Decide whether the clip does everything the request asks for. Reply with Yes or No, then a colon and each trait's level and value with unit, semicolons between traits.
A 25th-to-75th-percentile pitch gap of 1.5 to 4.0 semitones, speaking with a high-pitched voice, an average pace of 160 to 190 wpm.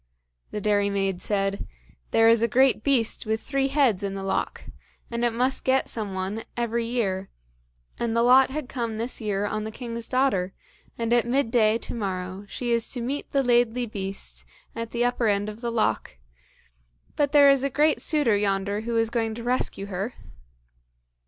Yes: average, 3.4 semitones; high, 230 Hz; average, 185 wpm